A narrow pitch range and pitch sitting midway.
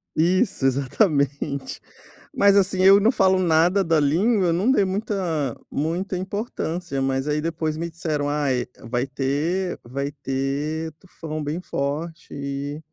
No: average, 4.7 semitones; medium, 160 Hz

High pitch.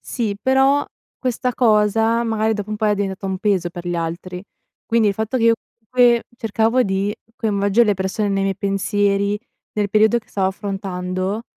Yes: high, 205 Hz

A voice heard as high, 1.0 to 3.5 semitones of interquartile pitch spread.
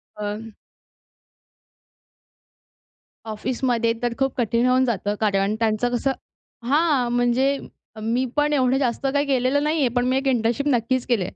Yes: high, 245 Hz; average, 2.8 semitones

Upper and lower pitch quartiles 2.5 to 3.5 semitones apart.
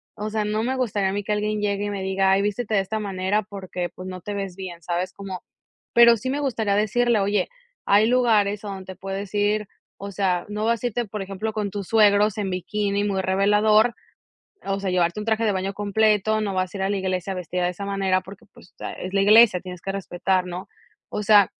No: narrow, 2.0 semitones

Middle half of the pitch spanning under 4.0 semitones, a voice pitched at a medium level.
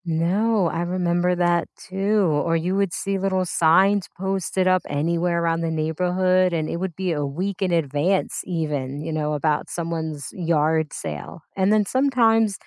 Yes: average, 3.1 semitones; medium, 175 Hz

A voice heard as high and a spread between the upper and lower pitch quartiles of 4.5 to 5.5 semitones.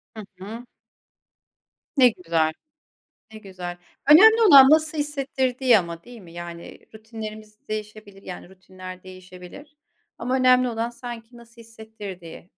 Yes: high, 220 Hz; average, 5.2 semitones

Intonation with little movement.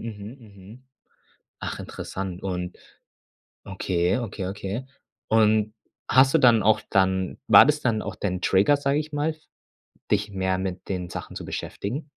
No: average, 5.1 semitones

